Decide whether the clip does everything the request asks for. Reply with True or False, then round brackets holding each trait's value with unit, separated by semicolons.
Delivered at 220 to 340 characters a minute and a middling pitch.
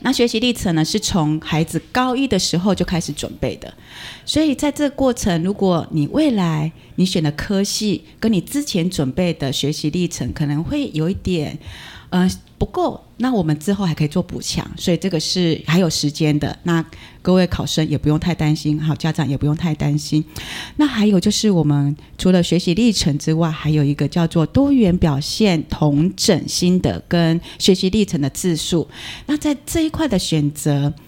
True (280 characters per minute; 170 Hz)